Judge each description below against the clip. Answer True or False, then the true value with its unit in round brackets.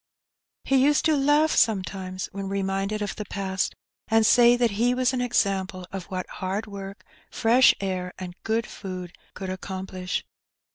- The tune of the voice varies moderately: True (3.9 semitones)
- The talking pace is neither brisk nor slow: True (155 wpm)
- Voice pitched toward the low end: False (200 Hz)